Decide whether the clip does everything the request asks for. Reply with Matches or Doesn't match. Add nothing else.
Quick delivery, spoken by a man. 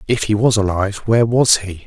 Matches